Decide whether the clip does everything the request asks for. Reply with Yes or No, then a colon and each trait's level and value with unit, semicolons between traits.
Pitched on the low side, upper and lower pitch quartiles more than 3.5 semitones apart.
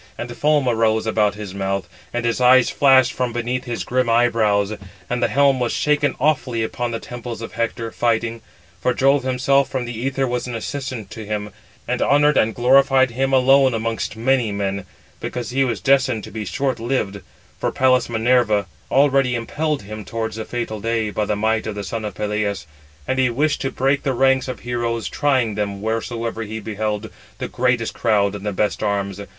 No: low, 120 Hz; average, 3.2 semitones